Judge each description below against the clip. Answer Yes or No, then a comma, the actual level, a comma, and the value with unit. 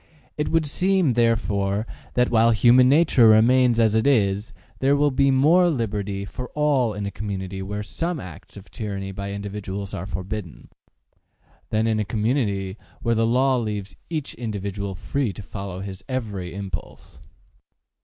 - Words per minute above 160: No, average, 155 wpm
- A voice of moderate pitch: No, low, 110 Hz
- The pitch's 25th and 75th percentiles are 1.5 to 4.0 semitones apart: No, average, 4.5 semitones